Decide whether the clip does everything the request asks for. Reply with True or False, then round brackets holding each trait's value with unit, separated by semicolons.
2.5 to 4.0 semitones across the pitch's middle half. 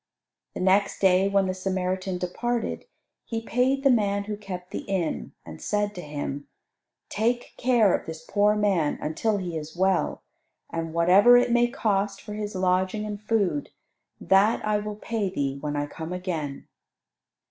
True (3.0 semitones)